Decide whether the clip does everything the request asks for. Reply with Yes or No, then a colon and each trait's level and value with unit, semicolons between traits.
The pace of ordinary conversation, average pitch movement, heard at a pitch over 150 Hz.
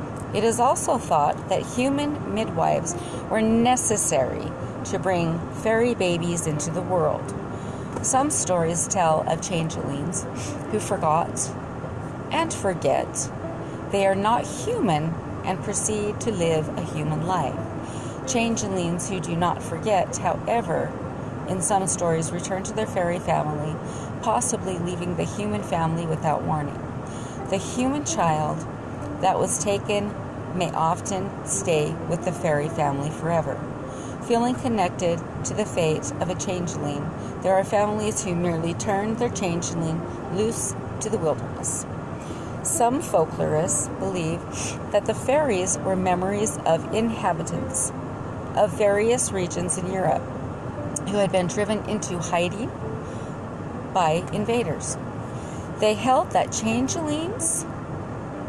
No: slow, 120 wpm; average, 4.6 semitones; medium, 185 Hz